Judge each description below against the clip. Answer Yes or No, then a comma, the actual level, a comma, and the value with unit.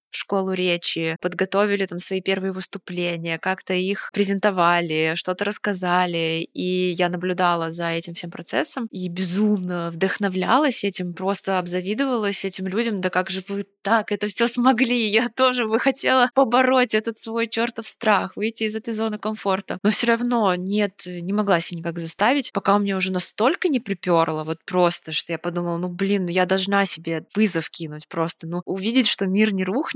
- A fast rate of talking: Yes, fast, 170 wpm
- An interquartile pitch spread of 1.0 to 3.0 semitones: No, average, 3.4 semitones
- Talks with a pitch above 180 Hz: Yes, high, 190 Hz